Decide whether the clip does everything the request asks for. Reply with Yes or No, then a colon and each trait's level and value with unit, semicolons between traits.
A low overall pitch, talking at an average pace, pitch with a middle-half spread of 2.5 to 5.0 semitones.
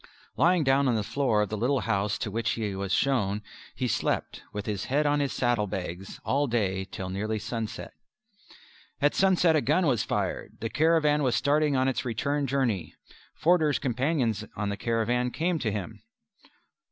No: low, 120 Hz; average, 175 wpm; wide, 5.4 semitones